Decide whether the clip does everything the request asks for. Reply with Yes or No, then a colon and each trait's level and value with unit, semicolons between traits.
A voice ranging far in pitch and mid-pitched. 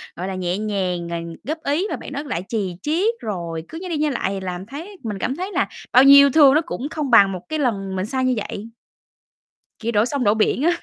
No: wide, 7.5 semitones; high, 235 Hz